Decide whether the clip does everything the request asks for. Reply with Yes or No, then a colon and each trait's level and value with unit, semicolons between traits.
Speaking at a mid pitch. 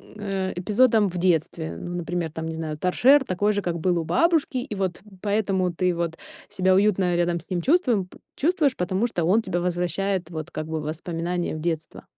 Yes: medium, 180 Hz